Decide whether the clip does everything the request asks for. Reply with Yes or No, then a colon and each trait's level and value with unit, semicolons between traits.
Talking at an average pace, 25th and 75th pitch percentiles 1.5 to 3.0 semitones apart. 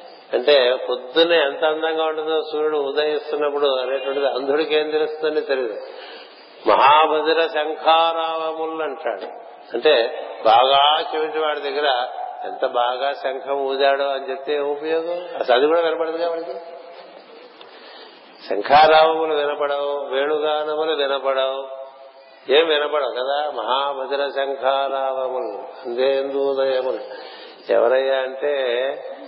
Yes: average, 90 wpm; narrow, 2.6 semitones